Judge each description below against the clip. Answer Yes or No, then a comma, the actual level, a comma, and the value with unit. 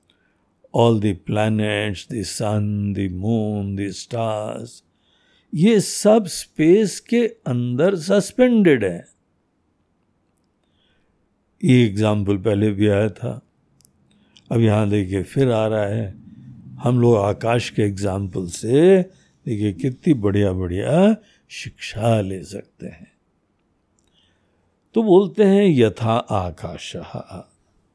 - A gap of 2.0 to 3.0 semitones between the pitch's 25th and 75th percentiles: No, average, 5.2 semitones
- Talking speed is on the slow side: Yes, slow, 90 wpm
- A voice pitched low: Yes, low, 105 Hz